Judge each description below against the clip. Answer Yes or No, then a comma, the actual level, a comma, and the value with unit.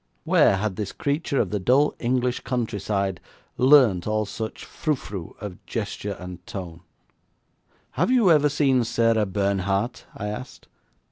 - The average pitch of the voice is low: Yes, low, 110 Hz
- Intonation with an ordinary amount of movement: Yes, average, 4.7 semitones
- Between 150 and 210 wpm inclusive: No, average, 140 wpm